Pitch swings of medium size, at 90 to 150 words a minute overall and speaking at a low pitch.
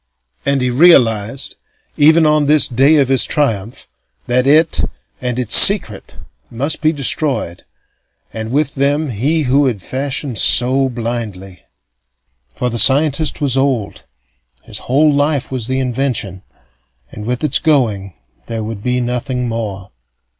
Yes: average, 3.8 semitones; average, 140 wpm; low, 130 Hz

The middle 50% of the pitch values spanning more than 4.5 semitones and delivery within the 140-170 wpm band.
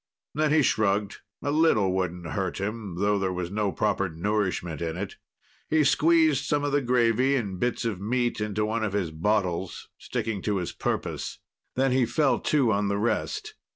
No: average, 5.2 semitones; average, 185 wpm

